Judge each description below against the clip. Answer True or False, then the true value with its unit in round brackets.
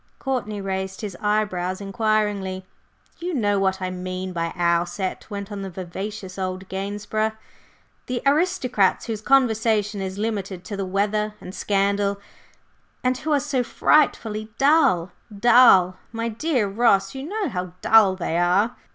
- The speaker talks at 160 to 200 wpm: False (145 wpm)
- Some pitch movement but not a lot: True (3.3 semitones)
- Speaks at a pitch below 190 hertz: False (205 Hz)